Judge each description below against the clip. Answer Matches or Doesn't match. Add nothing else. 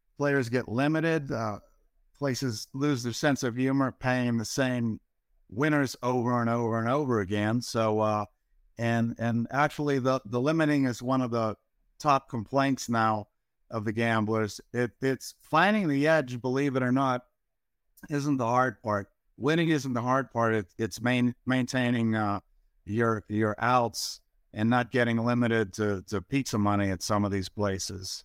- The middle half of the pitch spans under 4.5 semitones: Matches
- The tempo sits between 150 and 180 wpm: Matches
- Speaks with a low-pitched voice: Matches